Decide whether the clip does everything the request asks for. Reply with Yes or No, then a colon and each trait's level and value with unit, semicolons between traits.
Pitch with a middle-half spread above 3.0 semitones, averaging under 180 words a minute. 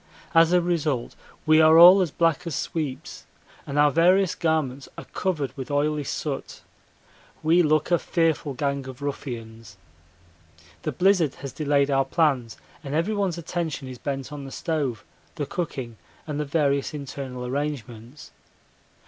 Yes: average, 3.4 semitones; average, 150 wpm